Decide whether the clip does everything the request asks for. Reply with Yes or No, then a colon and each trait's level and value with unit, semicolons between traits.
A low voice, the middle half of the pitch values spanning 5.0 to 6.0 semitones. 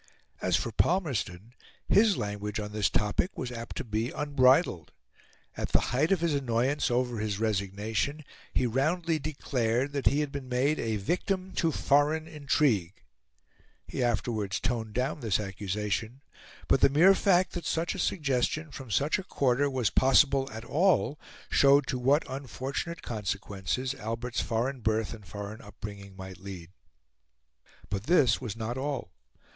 Yes: low, 125 Hz; average, 5.3 semitones